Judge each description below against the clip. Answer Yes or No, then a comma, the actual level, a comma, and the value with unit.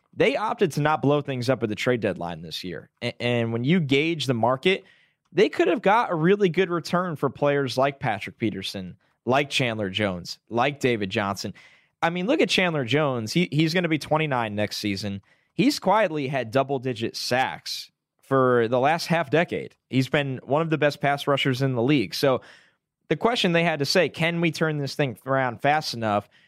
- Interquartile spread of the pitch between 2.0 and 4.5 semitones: No, average, 5.2 semitones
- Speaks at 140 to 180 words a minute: No, average, 200 wpm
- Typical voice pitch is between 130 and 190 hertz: Yes, medium, 140 Hz